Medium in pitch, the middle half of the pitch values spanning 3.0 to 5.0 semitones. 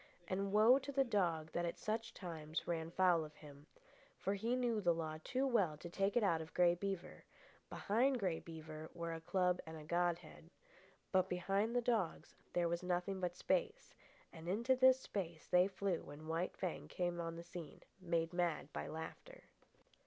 Yes: medium, 175 Hz; average, 3.7 semitones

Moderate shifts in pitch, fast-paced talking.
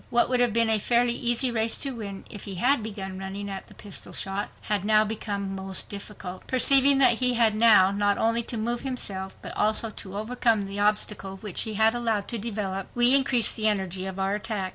Yes: average, 3.2 semitones; fast, 215 wpm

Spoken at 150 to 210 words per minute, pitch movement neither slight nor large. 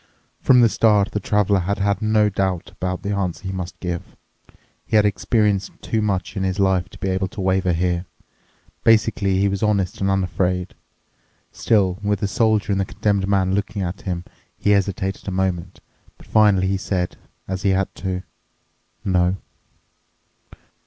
No: average, 170 wpm; narrow, 1.8 semitones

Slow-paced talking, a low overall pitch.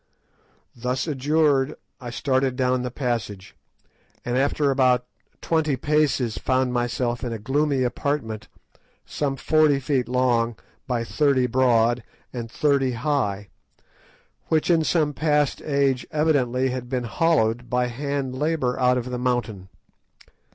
Yes: slow, 130 wpm; low, 130 Hz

